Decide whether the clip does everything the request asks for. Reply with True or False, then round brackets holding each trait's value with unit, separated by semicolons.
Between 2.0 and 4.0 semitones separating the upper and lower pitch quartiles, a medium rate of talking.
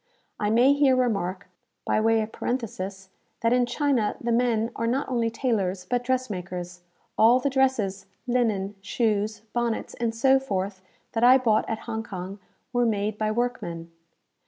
True (3.7 semitones; 160 wpm)